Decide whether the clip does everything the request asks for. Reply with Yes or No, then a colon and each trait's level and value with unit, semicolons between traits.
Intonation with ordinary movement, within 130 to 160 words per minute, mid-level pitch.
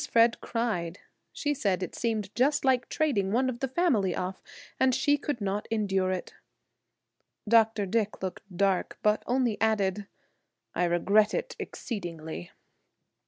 No: average, 4.4 semitones; average, 140 wpm; high, 215 Hz